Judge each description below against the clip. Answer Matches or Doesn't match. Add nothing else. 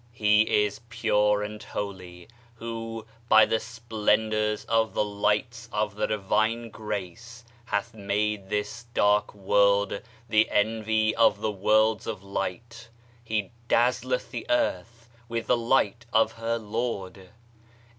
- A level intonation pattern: Matches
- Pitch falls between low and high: Doesn't match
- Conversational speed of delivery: Doesn't match